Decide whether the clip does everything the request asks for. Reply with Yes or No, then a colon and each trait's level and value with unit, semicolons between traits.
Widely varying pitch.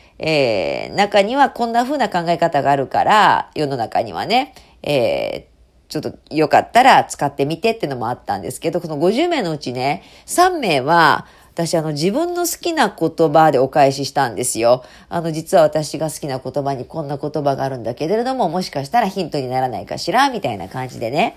Yes: wide, 6.3 semitones